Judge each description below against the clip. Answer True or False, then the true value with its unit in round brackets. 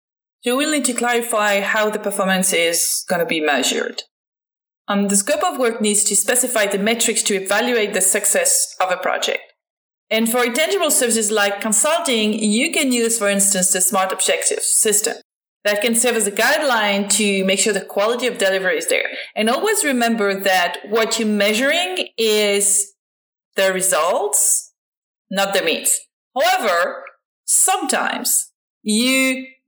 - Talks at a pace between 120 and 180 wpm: True (160 wpm)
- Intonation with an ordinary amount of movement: True (4.3 semitones)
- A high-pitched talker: True (220 Hz)